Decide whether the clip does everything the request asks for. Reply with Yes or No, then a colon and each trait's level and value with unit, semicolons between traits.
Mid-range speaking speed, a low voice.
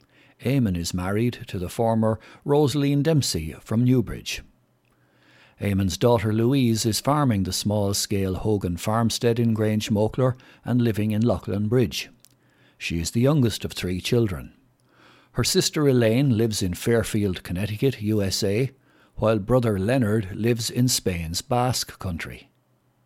No: slow, 130 wpm; low, 110 Hz